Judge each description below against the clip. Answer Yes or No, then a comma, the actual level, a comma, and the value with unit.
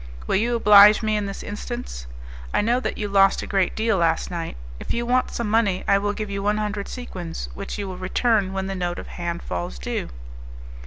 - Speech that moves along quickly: Yes, fast, 220 wpm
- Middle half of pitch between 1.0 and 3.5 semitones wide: Yes, average, 3.0 semitones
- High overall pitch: Yes, high, 200 Hz